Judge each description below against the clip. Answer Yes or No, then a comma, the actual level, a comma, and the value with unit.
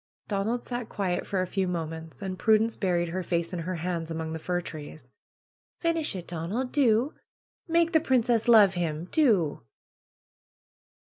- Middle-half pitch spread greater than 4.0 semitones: Yes, wide, 5.5 semitones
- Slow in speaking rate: No, average, 155 wpm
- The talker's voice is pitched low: No, medium, 185 Hz